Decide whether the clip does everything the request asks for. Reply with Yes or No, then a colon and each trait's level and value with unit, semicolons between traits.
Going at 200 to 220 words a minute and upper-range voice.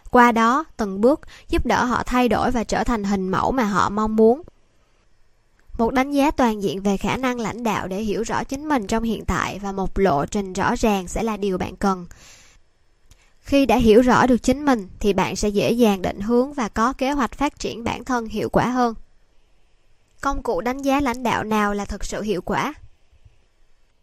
Yes: average, 210 wpm; high, 220 Hz